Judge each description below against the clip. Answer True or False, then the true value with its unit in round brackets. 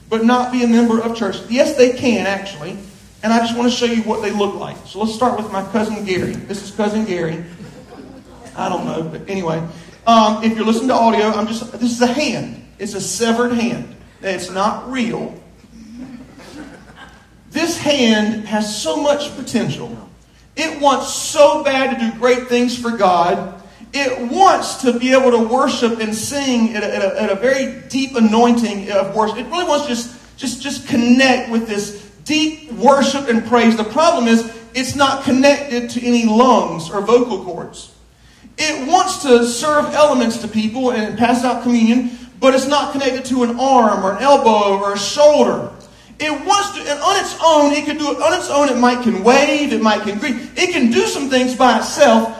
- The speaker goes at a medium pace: True (195 wpm)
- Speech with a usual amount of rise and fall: True (3.8 semitones)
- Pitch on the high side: True (240 Hz)